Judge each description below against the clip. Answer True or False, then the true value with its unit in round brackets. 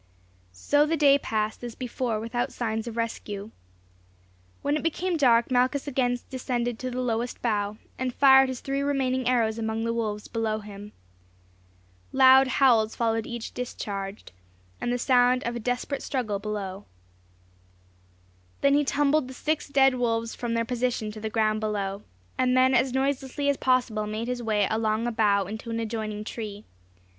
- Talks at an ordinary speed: True (165 wpm)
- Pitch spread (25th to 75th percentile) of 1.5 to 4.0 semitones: True (3.0 semitones)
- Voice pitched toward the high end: True (235 Hz)